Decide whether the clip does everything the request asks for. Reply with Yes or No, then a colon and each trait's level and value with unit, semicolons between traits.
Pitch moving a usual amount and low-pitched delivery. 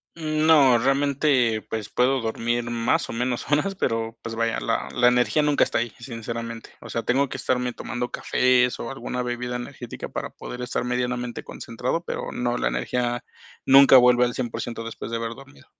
No: narrow, 1.9 semitones; low, 125 Hz